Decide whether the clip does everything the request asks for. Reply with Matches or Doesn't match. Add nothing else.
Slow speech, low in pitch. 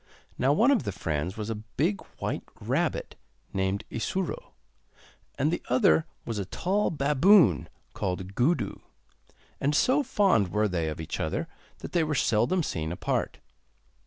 Doesn't match